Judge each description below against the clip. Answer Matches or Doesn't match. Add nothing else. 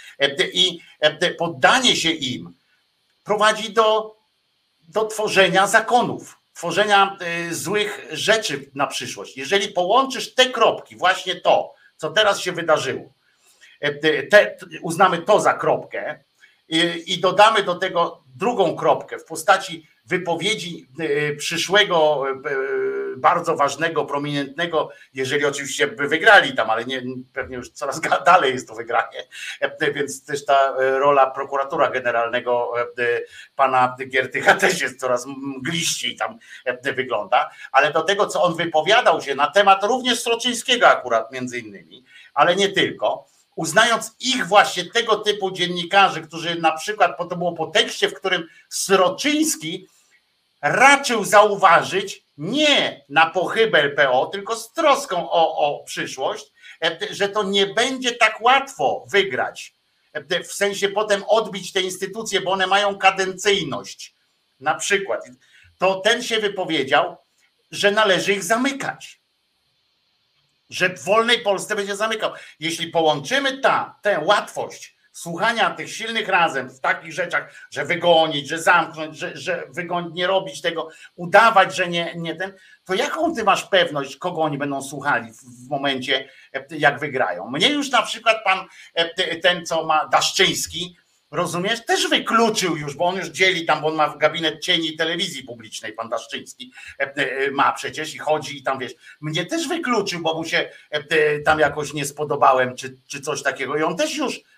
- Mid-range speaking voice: Matches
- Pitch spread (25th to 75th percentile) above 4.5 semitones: Matches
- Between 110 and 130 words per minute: Doesn't match